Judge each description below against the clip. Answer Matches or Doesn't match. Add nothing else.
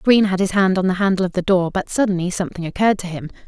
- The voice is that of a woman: Matches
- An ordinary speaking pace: Doesn't match